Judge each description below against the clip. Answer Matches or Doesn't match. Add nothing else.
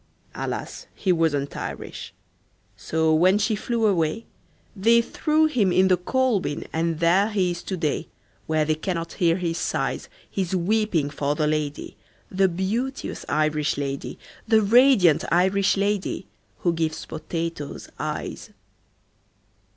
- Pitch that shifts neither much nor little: Matches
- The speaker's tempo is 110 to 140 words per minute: Matches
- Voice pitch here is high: Doesn't match